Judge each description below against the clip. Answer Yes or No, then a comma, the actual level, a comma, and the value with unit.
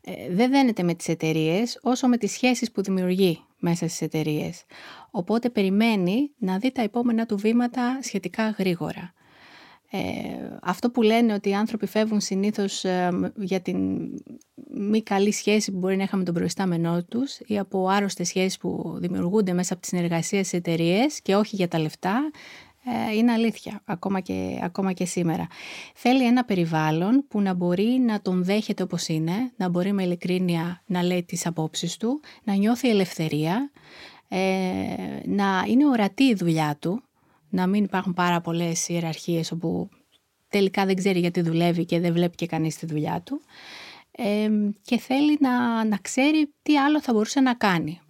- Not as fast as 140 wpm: No, average, 165 wpm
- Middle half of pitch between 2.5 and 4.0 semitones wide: No, average, 4.7 semitones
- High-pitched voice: Yes, high, 195 Hz